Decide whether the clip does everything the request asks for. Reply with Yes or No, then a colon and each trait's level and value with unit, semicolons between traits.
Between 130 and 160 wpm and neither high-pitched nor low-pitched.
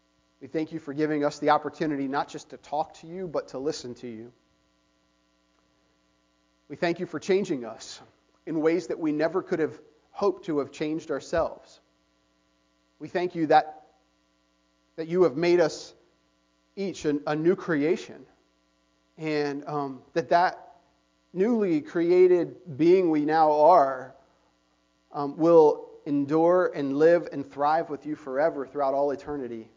Yes: average, 150 wpm; medium, 145 Hz